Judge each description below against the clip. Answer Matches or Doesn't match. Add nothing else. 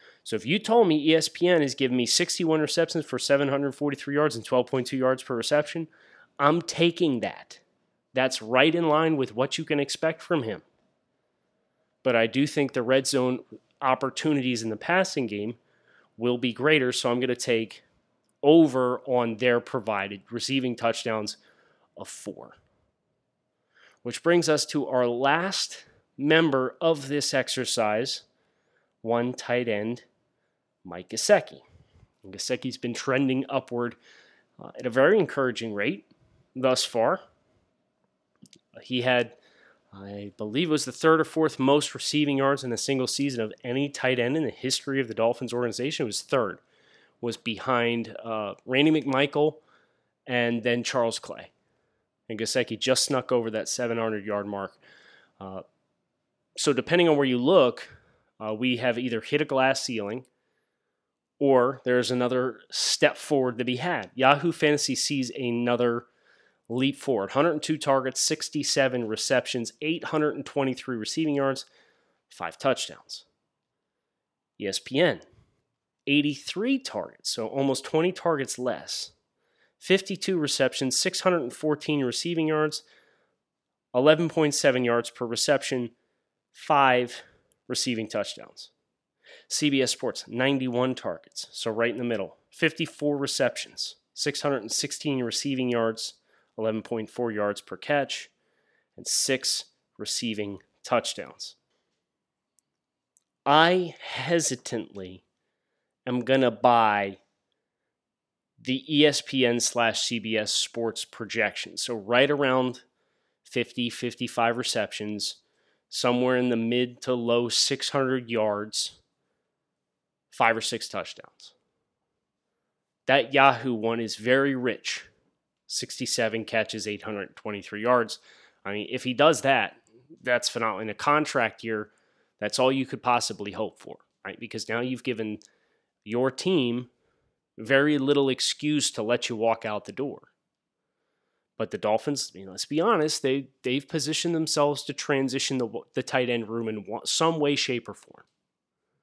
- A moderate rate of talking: Doesn't match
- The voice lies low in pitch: Matches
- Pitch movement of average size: Matches